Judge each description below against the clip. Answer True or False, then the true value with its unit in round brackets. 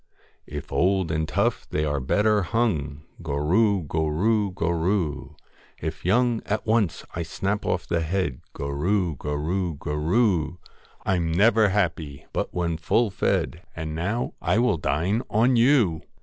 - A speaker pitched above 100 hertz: False (90 Hz)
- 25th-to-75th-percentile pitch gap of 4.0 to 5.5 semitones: True (5.1 semitones)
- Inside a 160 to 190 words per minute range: False (140 wpm)